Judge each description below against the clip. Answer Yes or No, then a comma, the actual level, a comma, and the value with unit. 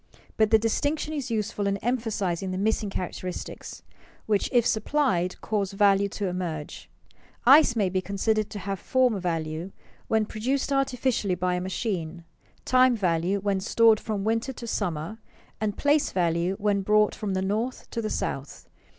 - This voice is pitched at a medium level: No, high, 205 Hz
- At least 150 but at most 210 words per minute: Yes, average, 160 wpm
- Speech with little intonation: No, average, 3.7 semitones